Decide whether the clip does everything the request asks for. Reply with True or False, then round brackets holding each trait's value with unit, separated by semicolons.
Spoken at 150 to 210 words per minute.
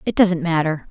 True (200 wpm)